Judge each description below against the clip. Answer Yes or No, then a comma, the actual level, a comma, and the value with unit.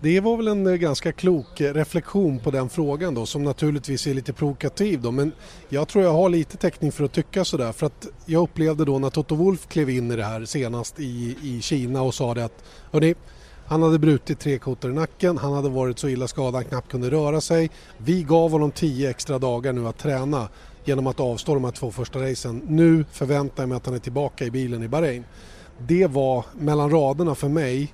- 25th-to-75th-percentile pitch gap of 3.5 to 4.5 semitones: Yes, average, 4.0 semitones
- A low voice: No, medium, 145 Hz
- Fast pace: Yes, fast, 225 wpm